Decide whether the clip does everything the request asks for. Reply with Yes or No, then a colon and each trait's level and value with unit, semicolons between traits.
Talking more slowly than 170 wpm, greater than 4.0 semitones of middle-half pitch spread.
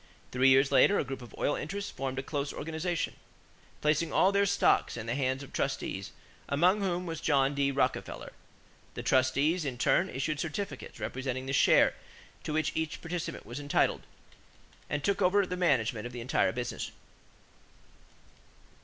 Yes: average, 160 wpm; average, 4.6 semitones